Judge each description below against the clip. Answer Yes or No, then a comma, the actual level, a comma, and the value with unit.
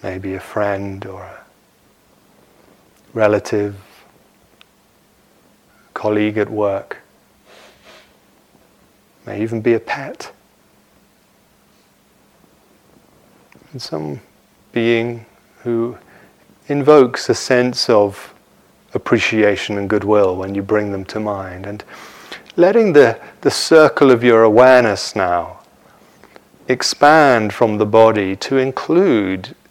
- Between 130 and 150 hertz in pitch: No, low, 105 Hz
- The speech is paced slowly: Yes, slow, 95 wpm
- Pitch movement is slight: No, average, 3.1 semitones